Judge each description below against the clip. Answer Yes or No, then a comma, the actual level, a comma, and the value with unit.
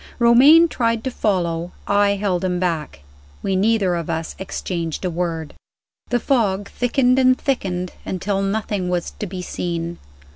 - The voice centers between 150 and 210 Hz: Yes, high, 190 Hz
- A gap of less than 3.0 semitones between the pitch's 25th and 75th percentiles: No, average, 4.6 semitones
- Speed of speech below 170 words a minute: Yes, average, 150 wpm